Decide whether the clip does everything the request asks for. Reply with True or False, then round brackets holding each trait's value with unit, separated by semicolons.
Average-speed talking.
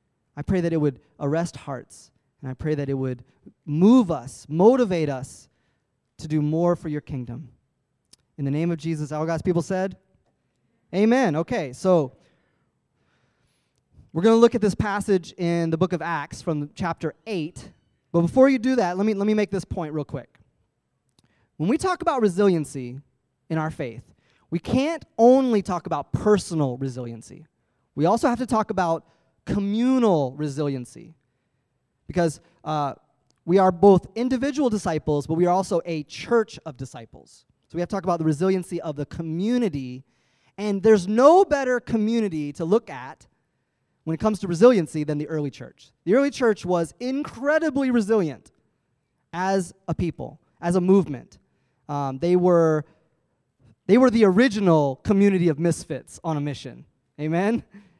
True (160 wpm)